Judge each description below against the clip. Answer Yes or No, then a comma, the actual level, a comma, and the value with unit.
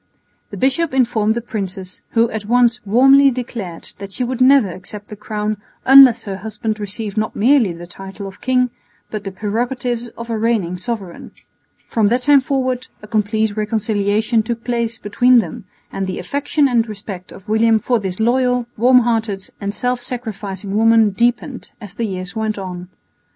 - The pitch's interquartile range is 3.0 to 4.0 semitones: Yes, average, 3.3 semitones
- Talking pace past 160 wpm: Yes, average, 170 wpm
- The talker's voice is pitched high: Yes, high, 220 Hz